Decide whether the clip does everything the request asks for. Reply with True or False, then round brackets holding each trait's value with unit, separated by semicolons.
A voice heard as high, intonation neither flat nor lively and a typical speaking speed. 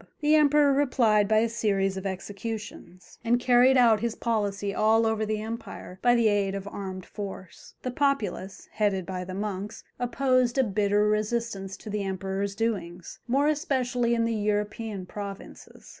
True (215 Hz; 3.2 semitones; 160 wpm)